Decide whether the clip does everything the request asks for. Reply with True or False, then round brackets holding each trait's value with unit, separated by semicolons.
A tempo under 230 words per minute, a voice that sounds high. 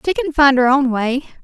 False (250 wpm; 275 Hz)